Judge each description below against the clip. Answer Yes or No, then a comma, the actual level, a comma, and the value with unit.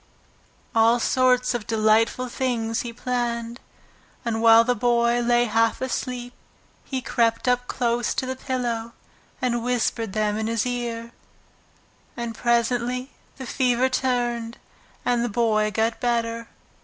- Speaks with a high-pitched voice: Yes, high, 235 Hz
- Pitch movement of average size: No, narrow, 1.5 semitones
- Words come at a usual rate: No, slow, 130 wpm